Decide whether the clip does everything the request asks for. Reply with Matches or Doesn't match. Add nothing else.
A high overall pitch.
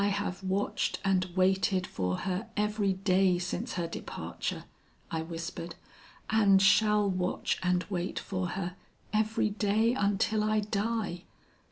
Matches